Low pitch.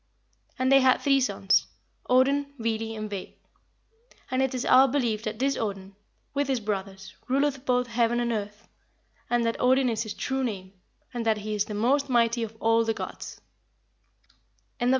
No: high, 235 Hz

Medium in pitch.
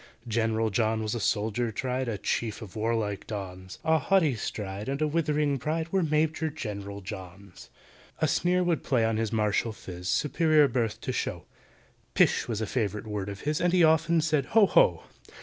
No: low, 115 Hz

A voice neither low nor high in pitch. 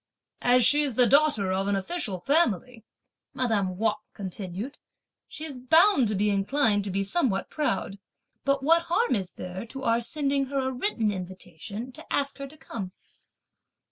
No: high, 235 Hz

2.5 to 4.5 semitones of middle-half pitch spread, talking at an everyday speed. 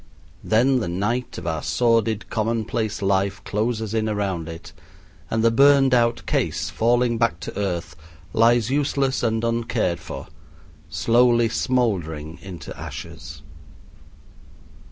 No: average, 3.7 semitones; slow, 120 wpm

